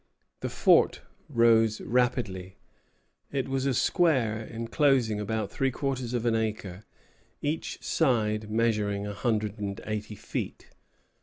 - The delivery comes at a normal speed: No, slow, 125 wpm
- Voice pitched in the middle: No, low, 115 Hz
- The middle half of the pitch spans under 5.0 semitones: Yes, average, 3.0 semitones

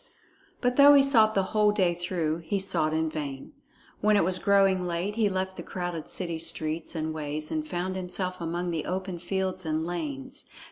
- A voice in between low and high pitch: Yes, medium, 180 Hz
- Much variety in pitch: No, average, 3.3 semitones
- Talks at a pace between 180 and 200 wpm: Yes, average, 190 wpm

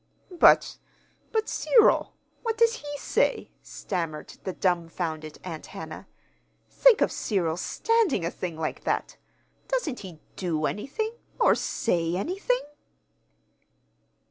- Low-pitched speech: No, high, 195 Hz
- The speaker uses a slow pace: Yes, slow, 115 wpm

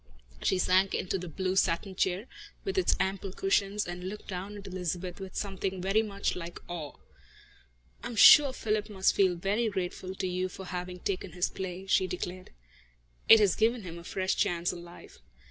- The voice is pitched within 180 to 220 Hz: Yes, high, 190 Hz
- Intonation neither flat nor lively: No, narrow, 1.7 semitones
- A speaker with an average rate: Yes, average, 185 wpm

